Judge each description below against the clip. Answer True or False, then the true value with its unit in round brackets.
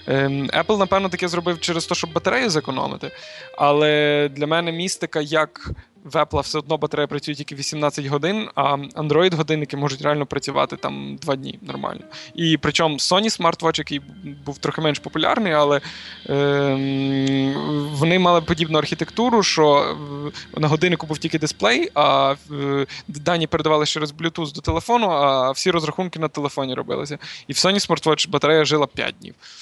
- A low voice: False (155 Hz)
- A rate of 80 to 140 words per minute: False (150 wpm)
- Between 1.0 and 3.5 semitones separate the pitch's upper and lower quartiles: True (2.7 semitones)